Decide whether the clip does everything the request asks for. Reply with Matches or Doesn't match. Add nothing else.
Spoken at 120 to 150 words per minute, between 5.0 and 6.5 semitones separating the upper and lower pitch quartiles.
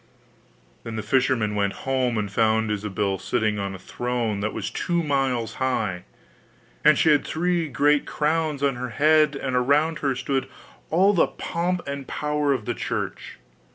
Doesn't match